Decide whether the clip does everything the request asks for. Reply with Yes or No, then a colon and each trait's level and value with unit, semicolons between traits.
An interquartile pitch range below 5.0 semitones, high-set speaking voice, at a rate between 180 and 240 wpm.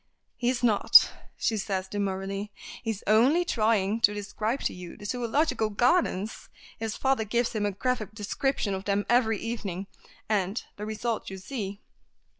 No: average, 3.1 semitones; high, 215 Hz; average, 155 wpm